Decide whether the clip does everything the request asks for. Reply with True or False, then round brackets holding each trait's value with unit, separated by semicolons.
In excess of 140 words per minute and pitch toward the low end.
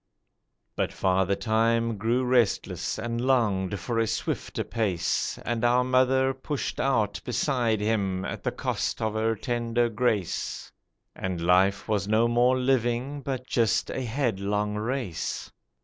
False (135 wpm; 115 Hz)